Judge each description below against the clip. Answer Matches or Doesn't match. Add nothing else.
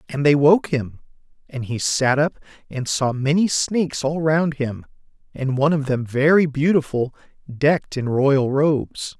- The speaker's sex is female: Doesn't match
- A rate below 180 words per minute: Matches